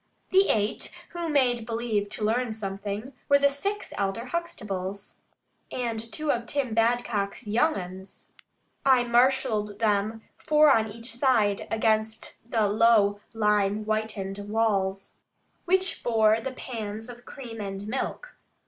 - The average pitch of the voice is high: Yes, high, 225 Hz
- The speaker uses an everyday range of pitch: Yes, average, 3.3 semitones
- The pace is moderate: No, slow, 130 wpm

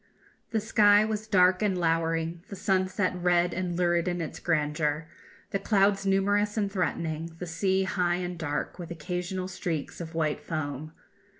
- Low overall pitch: No, medium, 180 Hz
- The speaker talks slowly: No, average, 160 wpm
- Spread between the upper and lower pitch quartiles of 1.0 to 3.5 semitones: Yes, average, 2.9 semitones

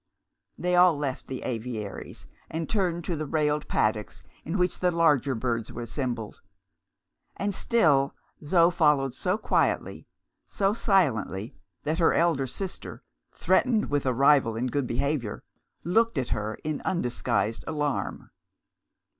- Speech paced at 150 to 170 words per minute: No, slow, 135 wpm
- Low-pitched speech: No, medium, 145 Hz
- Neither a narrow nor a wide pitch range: No, wide, 5.8 semitones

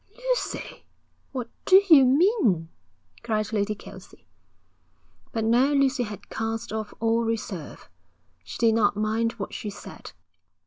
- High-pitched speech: Yes, high, 225 Hz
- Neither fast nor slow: No, slow, 130 wpm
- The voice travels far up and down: No, average, 3.6 semitones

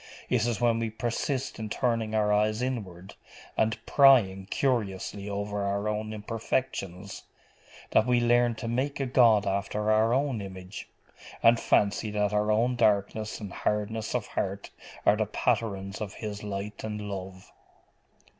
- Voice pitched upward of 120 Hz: No, low, 105 Hz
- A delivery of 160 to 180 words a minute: No, average, 150 wpm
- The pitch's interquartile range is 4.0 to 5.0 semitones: No, narrow, 2.5 semitones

